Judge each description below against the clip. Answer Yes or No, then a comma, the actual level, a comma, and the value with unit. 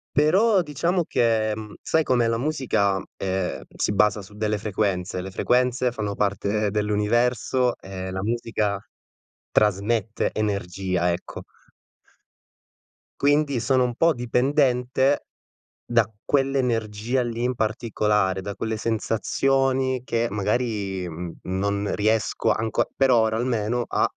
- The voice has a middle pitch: No, low, 110 Hz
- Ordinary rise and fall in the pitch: Yes, average, 3.6 semitones